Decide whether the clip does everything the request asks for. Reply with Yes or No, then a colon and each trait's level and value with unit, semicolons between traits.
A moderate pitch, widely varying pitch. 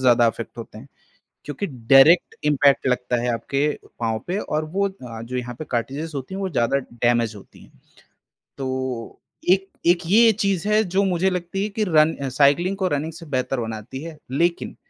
Yes: medium, 145 Hz; wide, 6.6 semitones